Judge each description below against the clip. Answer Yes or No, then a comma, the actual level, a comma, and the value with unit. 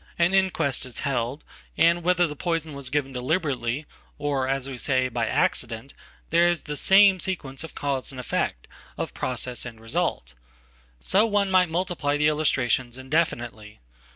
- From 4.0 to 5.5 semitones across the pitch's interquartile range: Yes, average, 5.0 semitones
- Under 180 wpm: Yes, average, 140 wpm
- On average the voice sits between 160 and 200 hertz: No, medium, 140 Hz